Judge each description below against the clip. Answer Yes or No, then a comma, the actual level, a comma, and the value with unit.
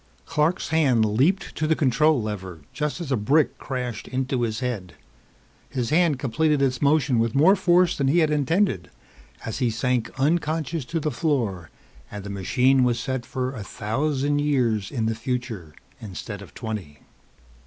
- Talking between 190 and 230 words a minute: No, average, 165 wpm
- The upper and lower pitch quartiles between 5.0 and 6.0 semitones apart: Yes, average, 5.3 semitones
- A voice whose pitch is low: Yes, low, 130 Hz